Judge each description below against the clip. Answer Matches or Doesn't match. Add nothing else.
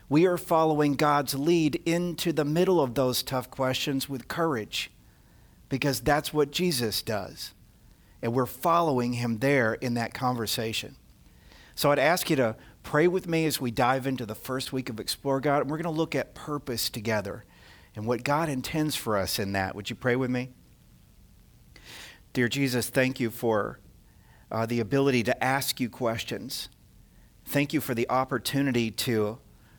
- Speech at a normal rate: Matches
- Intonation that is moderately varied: Matches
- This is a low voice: Matches